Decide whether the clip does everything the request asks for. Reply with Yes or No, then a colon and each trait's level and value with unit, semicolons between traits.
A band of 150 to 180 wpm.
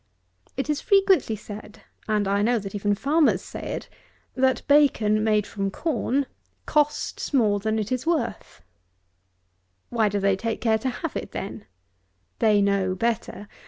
Yes: average, 155 wpm